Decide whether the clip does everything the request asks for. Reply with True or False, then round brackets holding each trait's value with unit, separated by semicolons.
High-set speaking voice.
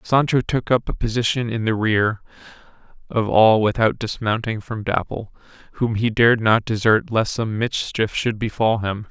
False (110 Hz)